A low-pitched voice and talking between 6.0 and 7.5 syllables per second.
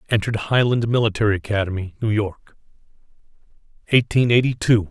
Yes: low, 110 Hz; 6.1 syllables/s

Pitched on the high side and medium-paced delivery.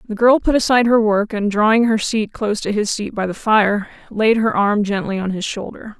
No: high, 215 Hz; fast, 240 wpm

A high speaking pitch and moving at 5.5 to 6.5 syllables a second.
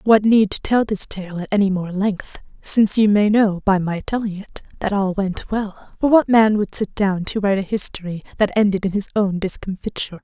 No: high, 200 Hz; 5.2 syllables/s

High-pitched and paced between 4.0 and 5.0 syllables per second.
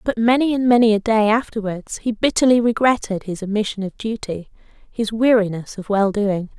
No: high, 215 Hz; 5.3 syllables/s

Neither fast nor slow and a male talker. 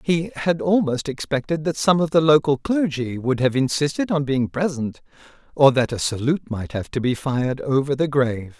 Yes: average, 195 wpm; male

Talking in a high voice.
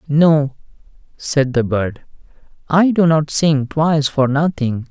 No: medium, 145 Hz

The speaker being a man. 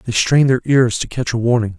Yes: male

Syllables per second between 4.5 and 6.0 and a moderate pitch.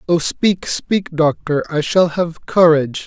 No: 3.9 syllables/s; medium, 165 Hz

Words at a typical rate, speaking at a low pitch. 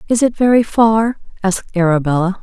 No: average, 150 wpm; high, 205 Hz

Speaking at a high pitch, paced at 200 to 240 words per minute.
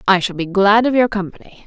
No: high, 205 Hz; fast, 250 wpm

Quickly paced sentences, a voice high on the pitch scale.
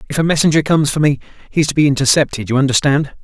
No: fast, 240 wpm; medium, 145 Hz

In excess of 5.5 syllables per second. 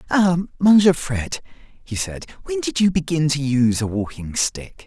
No: 4.5 syllables/s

